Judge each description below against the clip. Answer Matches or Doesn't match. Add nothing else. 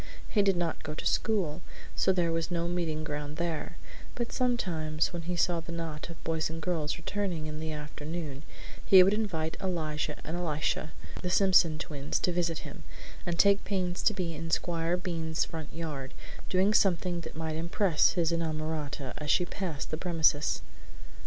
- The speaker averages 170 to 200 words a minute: Matches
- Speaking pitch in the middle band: Matches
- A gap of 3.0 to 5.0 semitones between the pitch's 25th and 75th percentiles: Doesn't match